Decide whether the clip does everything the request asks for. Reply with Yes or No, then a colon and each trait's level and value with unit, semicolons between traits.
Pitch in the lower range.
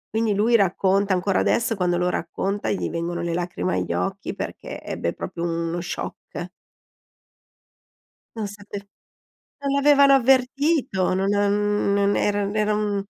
No: high, 200 Hz